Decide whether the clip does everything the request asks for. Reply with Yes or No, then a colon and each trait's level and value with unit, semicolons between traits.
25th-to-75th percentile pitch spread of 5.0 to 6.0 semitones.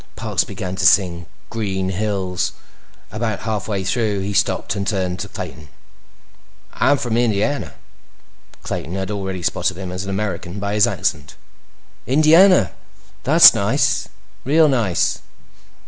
No: average, 3.2 semitones